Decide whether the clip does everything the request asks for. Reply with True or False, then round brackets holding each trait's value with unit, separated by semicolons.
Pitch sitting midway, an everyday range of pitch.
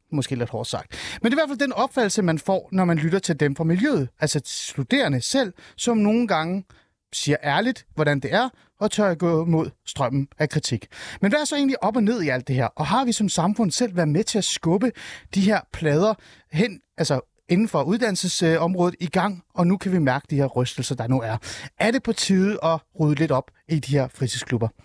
False (170 Hz; 6.9 semitones)